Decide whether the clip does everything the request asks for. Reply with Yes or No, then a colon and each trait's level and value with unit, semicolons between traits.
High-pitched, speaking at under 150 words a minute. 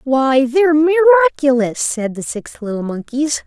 Yes: very high, 285 Hz; average, 140 wpm